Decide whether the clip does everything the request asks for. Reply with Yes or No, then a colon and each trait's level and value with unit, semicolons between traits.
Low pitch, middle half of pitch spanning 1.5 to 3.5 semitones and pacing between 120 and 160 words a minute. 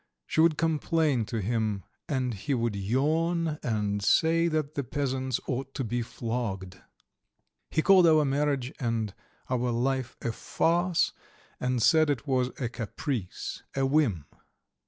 No: low, 130 Hz; average, 4.8 semitones; average, 140 wpm